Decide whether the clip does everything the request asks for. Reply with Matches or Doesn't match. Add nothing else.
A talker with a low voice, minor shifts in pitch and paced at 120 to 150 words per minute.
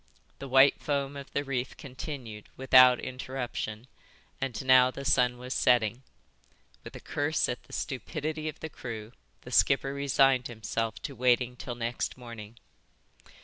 Matches